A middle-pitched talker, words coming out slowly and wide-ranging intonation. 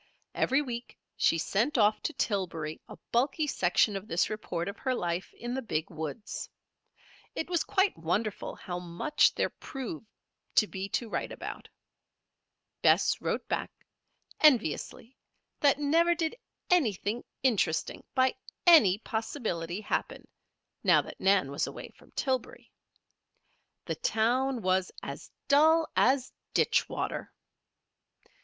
No: high, 225 Hz; slow, 130 wpm; wide, 6.8 semitones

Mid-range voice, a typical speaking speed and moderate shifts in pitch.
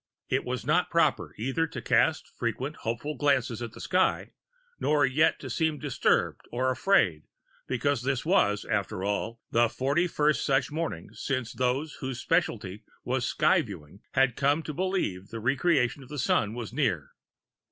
No: low, 130 Hz; average, 165 wpm; average, 4.6 semitones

